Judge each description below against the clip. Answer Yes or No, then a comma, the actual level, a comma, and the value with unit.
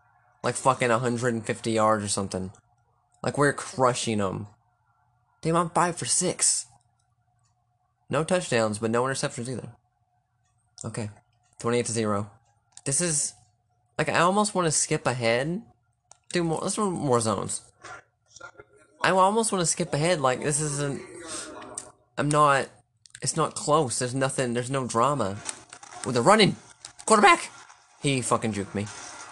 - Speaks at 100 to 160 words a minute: Yes, slow, 135 wpm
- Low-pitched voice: Yes, low, 120 Hz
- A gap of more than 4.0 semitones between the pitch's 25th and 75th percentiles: No, average, 3.7 semitones